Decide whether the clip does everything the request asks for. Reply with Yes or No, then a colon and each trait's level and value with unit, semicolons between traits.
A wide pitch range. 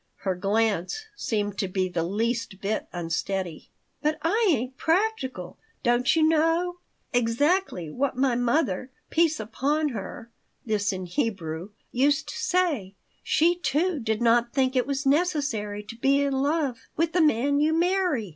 Yes: wide, 7.1 semitones